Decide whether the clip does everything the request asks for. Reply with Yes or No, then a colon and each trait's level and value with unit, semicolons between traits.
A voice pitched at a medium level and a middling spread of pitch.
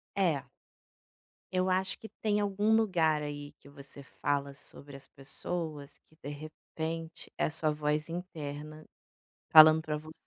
Yes: medium, 155 Hz; average, 3.2 semitones